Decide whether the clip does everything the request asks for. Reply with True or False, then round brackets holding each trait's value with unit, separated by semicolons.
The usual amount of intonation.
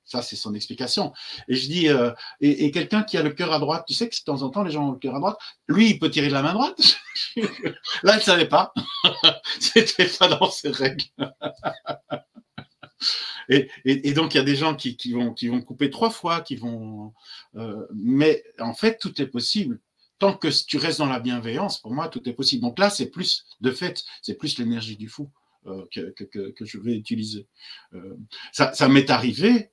False (7.2 semitones)